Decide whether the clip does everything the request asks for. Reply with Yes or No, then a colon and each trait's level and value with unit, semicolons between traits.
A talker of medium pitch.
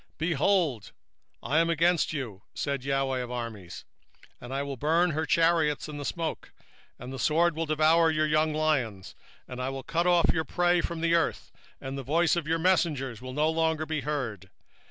Yes: medium, 155 Hz